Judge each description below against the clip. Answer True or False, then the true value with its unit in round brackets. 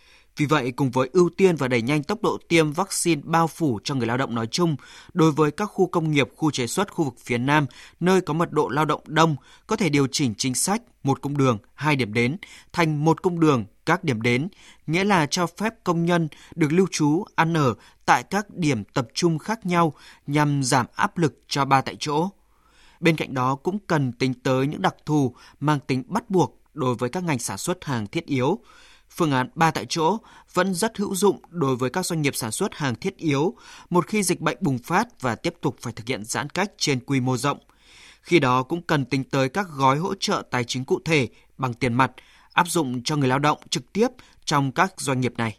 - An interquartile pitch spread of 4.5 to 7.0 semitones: True (4.8 semitones)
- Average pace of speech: True (230 wpm)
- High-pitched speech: False (150 Hz)